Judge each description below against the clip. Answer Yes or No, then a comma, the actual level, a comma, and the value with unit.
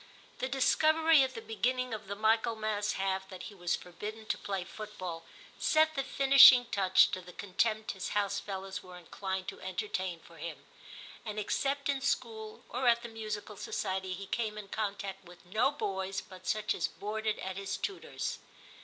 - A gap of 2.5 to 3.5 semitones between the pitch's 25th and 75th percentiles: Yes, average, 3.2 semitones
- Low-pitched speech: No, high, 210 Hz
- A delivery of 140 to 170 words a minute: No, average, 185 wpm